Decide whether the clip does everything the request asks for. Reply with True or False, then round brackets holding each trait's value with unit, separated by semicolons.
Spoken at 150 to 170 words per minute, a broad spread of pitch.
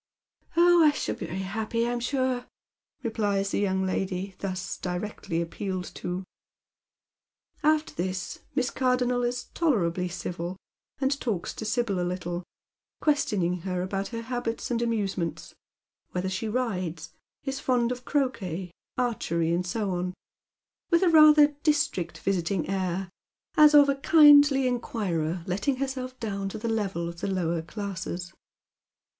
False (140 wpm; 5.8 semitones)